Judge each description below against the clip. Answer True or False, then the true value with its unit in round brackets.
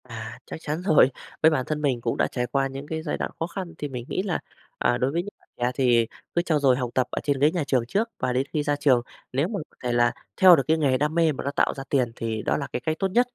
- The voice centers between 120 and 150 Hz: True (140 Hz)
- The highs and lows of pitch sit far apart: False (4.1 semitones)